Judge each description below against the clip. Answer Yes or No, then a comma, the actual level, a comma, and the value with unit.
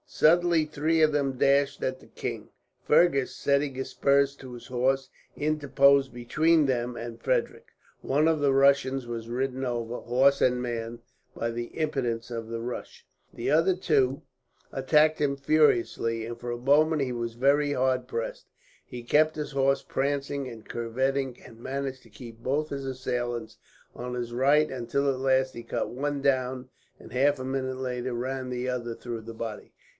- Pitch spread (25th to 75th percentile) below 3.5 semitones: Yes, average, 2.7 semitones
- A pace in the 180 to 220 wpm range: No, average, 170 wpm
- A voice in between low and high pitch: No, low, 130 Hz